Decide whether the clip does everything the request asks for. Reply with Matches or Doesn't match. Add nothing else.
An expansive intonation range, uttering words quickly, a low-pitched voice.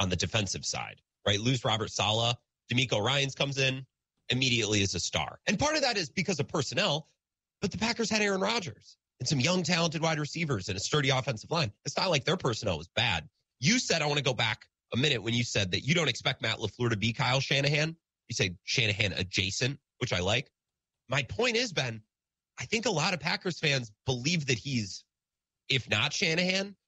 Matches